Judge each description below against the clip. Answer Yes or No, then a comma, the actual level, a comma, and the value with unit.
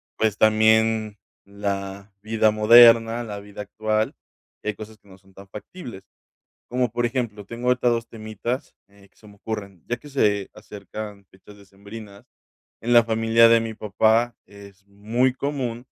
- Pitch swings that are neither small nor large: No, narrow, 2.3 semitones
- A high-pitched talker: No, low, 110 Hz